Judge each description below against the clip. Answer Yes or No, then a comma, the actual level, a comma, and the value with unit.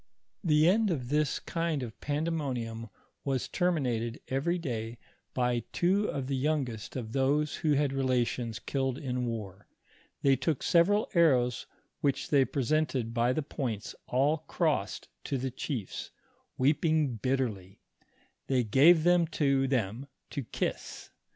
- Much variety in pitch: No, average, 4.0 semitones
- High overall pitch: No, low, 135 Hz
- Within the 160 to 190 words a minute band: No, average, 145 wpm